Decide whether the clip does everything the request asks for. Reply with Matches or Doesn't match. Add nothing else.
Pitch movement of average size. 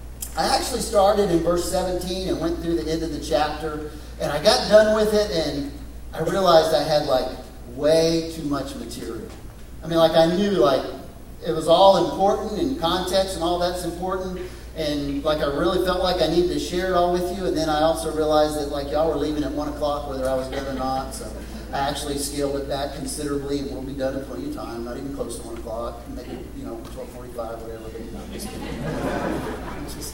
Matches